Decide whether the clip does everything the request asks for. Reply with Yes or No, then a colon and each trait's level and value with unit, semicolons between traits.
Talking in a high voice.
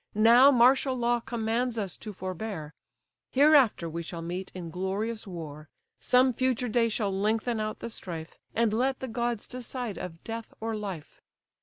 Yes: high, 220 Hz